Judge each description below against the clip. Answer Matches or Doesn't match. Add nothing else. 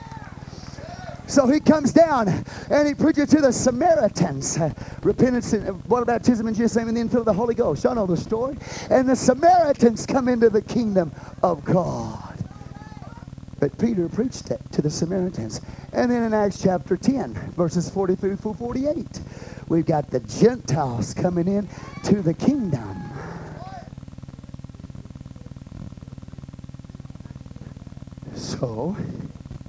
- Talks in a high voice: Matches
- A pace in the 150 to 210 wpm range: Doesn't match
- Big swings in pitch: Matches